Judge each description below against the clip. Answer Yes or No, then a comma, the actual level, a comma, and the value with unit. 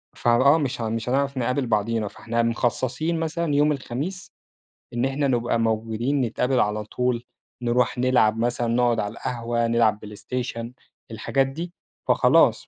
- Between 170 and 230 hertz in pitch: No, low, 120 Hz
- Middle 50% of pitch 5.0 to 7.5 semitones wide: No, average, 2.7 semitones